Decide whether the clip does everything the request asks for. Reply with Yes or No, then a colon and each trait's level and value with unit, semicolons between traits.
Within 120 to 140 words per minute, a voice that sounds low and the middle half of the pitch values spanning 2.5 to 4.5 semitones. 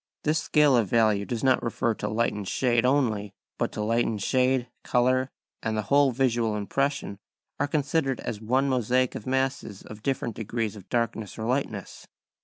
No: average, 175 wpm; low, 120 Hz; average, 3.5 semitones